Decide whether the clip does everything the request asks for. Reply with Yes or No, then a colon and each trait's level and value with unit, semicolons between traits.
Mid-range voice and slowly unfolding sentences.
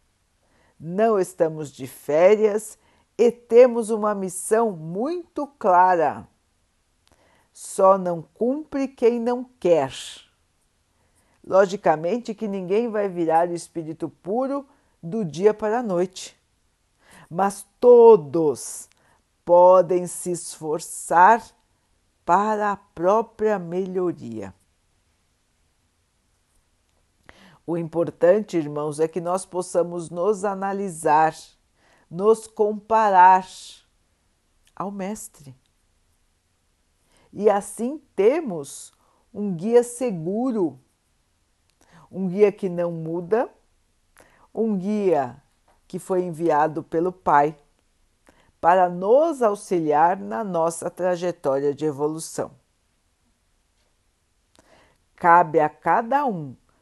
Yes: medium, 175 Hz; slow, 85 wpm